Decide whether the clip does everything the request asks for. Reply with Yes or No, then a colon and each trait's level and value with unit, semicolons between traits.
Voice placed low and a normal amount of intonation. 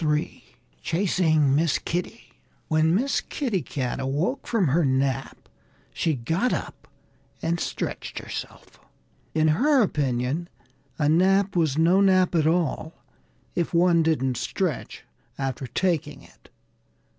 No: medium, 160 Hz; average, 4.2 semitones